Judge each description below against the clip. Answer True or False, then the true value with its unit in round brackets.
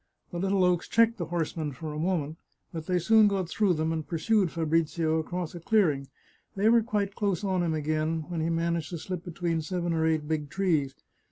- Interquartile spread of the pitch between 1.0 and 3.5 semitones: True (3.0 semitones)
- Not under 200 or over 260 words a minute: True (205 wpm)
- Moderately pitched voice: True (170 Hz)